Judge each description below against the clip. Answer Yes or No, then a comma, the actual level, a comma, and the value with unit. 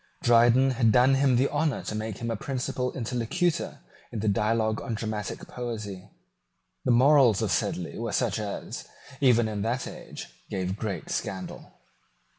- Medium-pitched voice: No, low, 115 Hz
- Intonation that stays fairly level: No, average, 3.0 semitones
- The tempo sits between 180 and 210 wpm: No, average, 155 wpm